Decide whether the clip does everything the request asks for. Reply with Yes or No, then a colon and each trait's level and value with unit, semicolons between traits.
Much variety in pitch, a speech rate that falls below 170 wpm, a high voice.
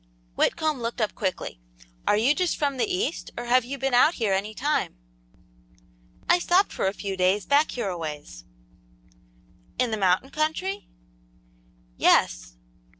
Yes: wide, 7.2 semitones; average, 150 wpm; high, 235 Hz